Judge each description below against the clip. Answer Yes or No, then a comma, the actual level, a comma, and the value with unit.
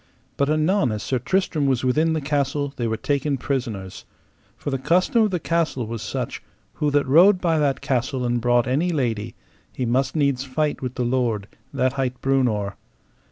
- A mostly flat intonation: No, average, 3.7 semitones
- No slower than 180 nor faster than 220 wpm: Yes, average, 185 wpm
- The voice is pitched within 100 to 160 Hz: Yes, low, 135 Hz